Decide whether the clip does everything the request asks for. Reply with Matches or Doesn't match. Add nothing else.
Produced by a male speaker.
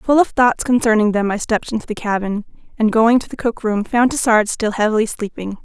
Doesn't match